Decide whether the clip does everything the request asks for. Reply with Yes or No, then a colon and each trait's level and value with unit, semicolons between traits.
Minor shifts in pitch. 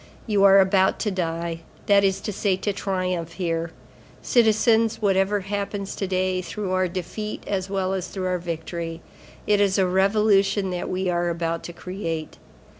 Yes: narrow, 2.3 semitones